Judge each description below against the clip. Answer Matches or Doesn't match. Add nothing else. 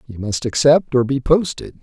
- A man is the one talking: Matches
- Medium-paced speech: Matches